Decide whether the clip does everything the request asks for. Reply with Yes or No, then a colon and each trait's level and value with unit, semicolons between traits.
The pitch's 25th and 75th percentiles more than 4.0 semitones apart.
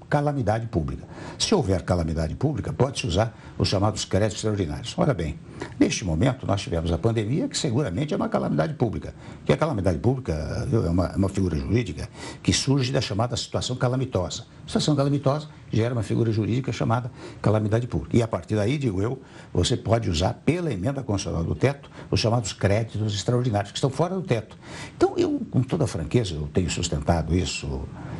Yes: average, 5.2 semitones